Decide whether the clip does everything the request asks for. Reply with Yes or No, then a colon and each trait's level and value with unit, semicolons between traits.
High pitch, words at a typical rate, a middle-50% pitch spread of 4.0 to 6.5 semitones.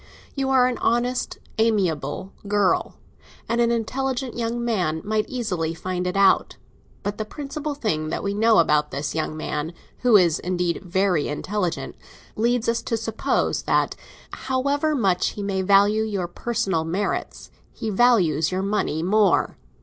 Yes: high, 205 Hz; average, 145 wpm; average, 5.0 semitones